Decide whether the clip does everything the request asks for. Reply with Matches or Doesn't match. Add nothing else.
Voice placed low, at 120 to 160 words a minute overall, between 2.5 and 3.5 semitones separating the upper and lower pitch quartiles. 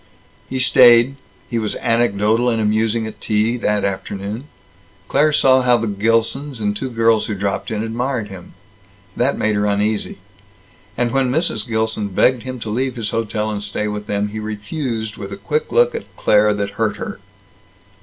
Doesn't match